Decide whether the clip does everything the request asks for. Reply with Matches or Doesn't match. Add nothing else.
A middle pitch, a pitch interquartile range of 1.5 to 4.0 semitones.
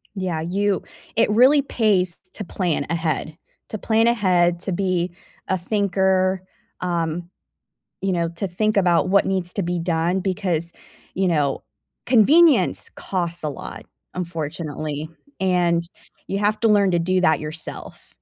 Matches